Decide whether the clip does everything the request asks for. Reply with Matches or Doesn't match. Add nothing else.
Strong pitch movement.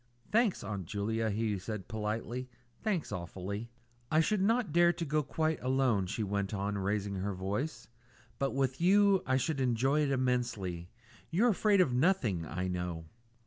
Matches